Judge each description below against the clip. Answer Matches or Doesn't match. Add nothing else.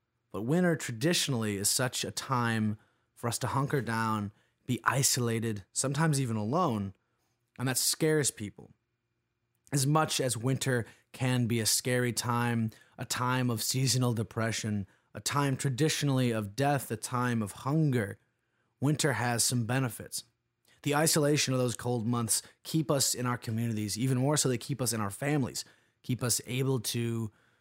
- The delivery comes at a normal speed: Matches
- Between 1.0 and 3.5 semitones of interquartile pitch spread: Matches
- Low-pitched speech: Matches